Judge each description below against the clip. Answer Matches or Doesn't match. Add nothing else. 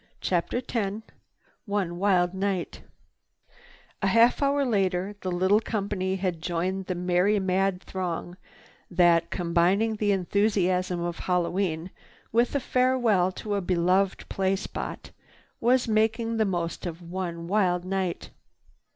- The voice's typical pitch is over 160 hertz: Matches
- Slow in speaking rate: Matches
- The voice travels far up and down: Doesn't match